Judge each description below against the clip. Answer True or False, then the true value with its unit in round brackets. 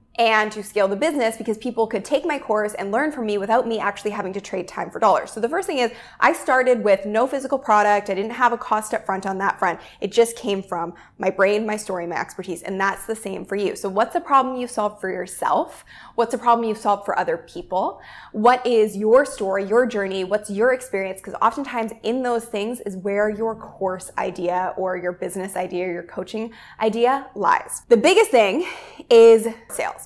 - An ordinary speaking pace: False (220 wpm)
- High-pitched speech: True (215 Hz)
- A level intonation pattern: False (3.3 semitones)